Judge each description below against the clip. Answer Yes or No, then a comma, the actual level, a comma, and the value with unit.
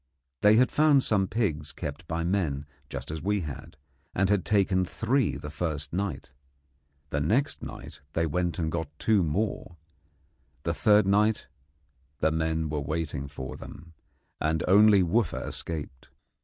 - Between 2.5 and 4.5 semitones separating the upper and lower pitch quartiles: No, average, 5.1 semitones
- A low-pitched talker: Yes, very low, 85 Hz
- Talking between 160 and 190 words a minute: No, average, 150 wpm